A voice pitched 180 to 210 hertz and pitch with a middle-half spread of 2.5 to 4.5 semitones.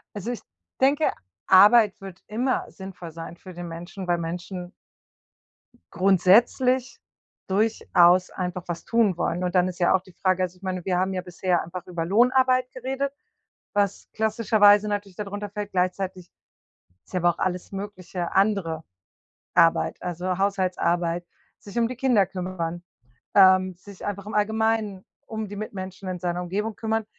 Yes: high, 190 Hz; average, 2.8 semitones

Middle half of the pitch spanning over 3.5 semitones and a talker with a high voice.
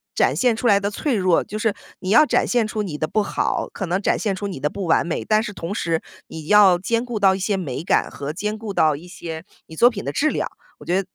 Yes: average, 4.1 semitones; high, 195 Hz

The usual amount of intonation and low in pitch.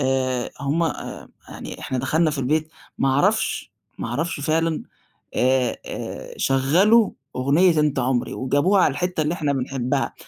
No: average, 3.7 semitones; medium, 145 Hz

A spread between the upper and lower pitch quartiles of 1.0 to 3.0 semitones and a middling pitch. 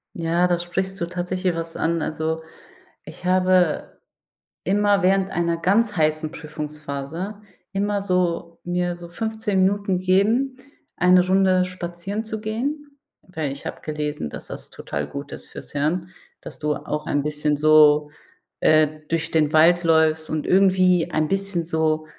No: average, 3.5 semitones; medium, 175 Hz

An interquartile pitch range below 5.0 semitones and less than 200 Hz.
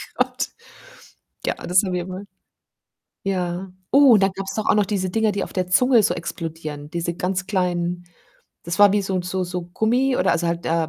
Yes: average, 2.7 semitones; medium, 185 Hz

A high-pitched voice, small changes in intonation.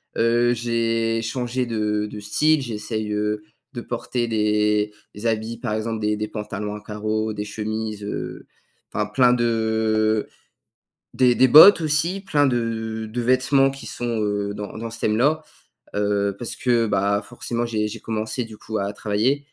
No: low, 110 Hz; narrow, 2.3 semitones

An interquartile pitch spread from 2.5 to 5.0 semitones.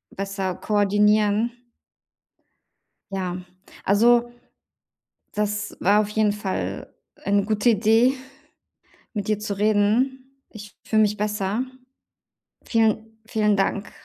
No: narrow, 1.5 semitones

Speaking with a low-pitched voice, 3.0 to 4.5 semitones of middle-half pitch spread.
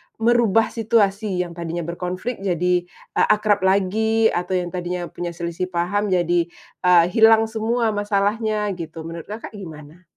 No: high, 190 Hz; average, 3.7 semitones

